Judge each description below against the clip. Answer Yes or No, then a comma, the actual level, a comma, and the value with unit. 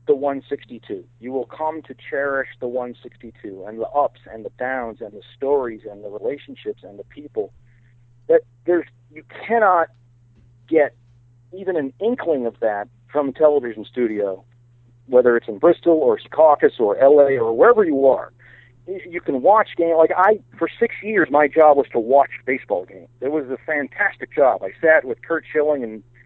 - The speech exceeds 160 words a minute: Yes, average, 175 wpm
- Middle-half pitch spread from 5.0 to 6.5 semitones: Yes, wide, 5.4 semitones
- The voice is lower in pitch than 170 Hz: Yes, medium, 140 Hz